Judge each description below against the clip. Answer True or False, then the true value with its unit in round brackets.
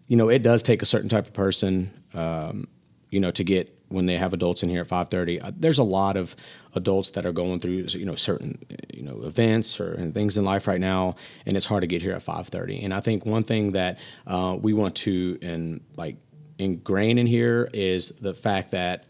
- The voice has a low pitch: True (95 Hz)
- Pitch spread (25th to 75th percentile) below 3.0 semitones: False (3.3 semitones)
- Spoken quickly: True (225 wpm)